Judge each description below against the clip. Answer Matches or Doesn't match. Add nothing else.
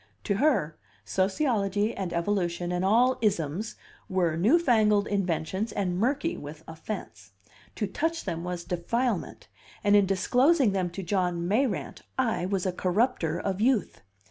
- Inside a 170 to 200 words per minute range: Doesn't match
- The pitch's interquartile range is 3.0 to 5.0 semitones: Matches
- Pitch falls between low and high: Doesn't match